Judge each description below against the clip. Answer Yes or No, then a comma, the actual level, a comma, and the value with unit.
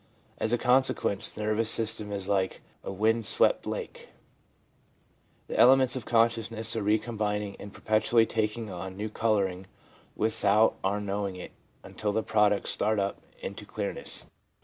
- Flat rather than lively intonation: Yes, narrow, 1.9 semitones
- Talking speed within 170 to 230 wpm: No, average, 155 wpm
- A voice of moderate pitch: No, low, 110 Hz